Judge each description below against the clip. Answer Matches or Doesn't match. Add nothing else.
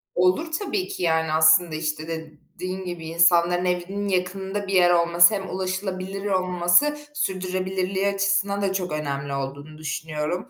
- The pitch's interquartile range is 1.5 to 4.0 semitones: Matches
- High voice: Doesn't match